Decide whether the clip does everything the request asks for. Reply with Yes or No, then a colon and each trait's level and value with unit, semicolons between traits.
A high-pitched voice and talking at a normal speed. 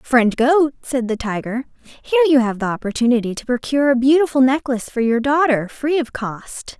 Yes: very high, 260 Hz; average, 185 wpm